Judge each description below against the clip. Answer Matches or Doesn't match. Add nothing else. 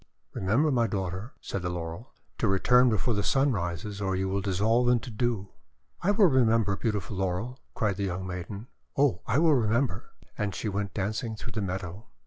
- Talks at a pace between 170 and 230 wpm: Matches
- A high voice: Doesn't match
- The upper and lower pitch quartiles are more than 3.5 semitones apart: Matches